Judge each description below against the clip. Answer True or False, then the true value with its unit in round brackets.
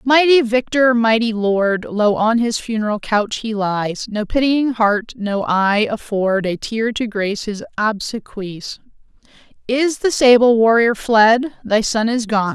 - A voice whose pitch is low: False (225 Hz)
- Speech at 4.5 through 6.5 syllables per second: False (3.9 syllables/s)